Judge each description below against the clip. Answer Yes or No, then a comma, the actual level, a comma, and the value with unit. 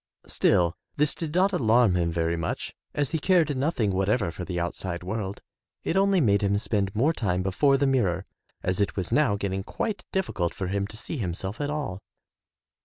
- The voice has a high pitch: No, low, 100 Hz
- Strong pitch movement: Yes, wide, 7.6 semitones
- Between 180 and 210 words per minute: Yes, average, 190 wpm